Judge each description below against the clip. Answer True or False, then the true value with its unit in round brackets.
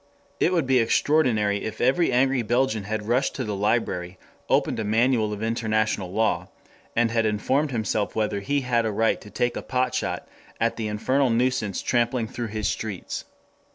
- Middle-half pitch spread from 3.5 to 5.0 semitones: False (3.0 semitones)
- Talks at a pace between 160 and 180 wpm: True (170 wpm)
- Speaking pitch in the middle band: False (115 Hz)